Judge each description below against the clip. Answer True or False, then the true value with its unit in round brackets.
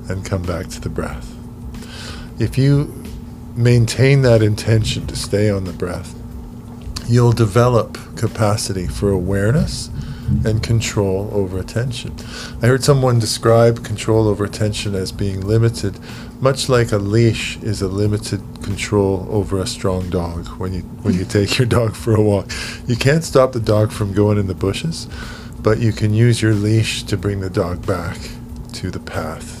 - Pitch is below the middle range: True (110 Hz)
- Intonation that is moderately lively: True (3.1 semitones)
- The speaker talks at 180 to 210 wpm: False (165 wpm)